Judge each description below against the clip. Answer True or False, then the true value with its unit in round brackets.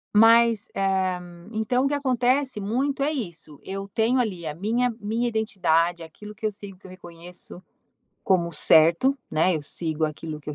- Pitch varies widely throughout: True (5.8 semitones)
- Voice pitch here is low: False (205 Hz)